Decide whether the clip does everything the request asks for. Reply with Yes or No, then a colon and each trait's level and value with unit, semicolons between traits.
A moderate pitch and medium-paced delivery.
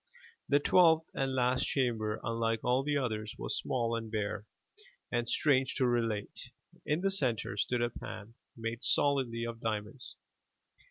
No: low, 120 Hz; average, 150 wpm